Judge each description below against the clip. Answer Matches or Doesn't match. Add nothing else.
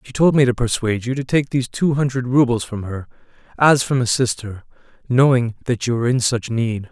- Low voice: Matches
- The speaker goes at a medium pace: Doesn't match